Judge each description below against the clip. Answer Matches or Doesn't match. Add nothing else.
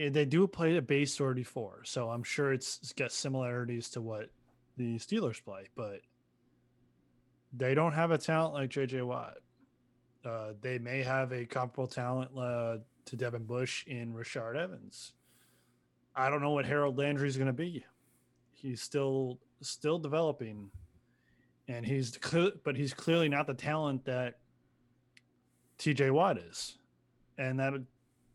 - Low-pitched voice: Matches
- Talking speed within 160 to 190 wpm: Doesn't match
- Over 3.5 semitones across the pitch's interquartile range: Doesn't match